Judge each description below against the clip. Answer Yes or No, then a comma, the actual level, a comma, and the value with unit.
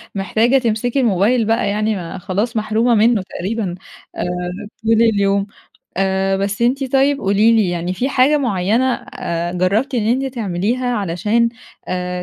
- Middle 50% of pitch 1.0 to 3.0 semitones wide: No, average, 3.8 semitones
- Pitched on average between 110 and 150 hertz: No, high, 215 Hz